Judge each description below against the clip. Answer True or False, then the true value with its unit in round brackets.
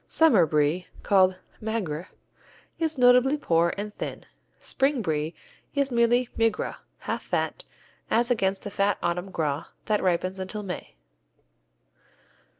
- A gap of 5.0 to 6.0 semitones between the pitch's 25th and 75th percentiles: True (5.5 semitones)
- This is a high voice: True (200 Hz)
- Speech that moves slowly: True (125 wpm)